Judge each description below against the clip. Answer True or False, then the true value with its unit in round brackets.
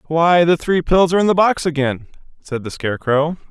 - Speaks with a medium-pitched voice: True (160 Hz)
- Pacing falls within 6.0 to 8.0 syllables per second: False (5.5 syllables/s)